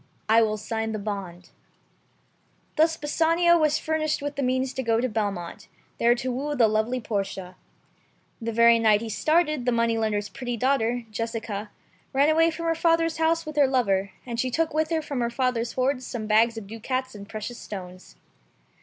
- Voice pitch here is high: Yes, high, 240 Hz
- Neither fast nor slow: Yes, average, 185 wpm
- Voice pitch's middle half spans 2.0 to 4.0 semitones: No, average, 5.1 semitones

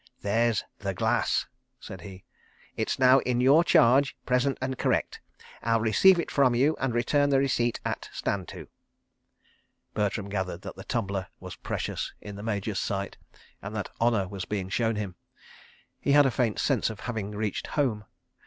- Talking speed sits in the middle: Yes, average, 170 wpm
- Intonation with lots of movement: No, average, 4.4 semitones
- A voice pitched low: Yes, low, 115 Hz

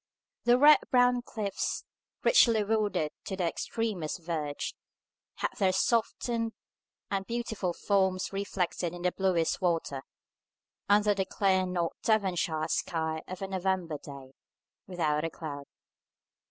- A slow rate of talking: Yes, slow, 125 wpm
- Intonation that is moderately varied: Yes, average, 4.1 semitones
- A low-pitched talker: No, high, 190 Hz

